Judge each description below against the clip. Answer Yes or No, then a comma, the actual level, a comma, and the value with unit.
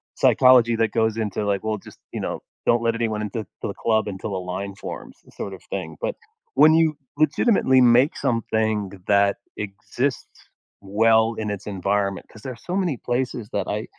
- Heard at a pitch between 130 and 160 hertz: No, low, 110 Hz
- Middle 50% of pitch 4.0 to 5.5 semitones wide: No, average, 3.3 semitones